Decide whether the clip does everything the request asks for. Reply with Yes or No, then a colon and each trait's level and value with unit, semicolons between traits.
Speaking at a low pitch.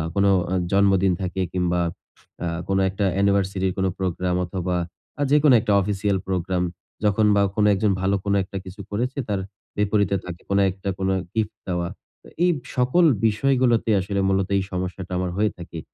Yes: very low, 95 Hz